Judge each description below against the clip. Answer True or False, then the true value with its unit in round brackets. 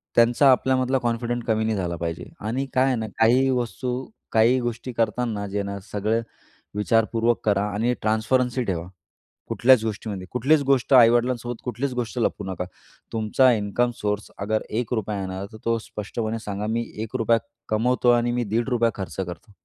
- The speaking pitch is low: True (115 Hz)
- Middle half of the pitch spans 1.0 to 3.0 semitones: True (2.6 semitones)